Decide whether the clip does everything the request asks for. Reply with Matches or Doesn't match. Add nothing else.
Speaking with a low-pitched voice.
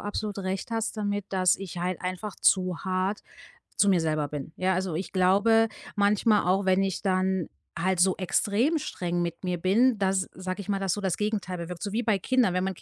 Doesn't match